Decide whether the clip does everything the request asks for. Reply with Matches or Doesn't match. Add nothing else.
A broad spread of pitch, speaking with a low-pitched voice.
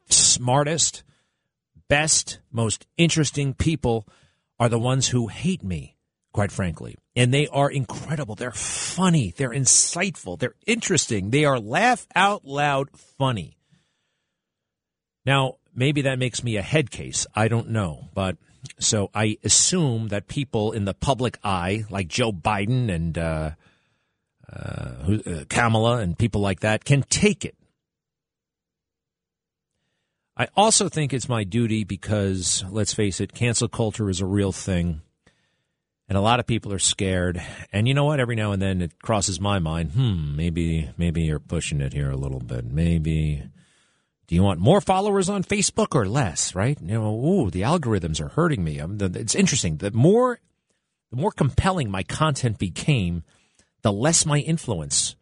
Matches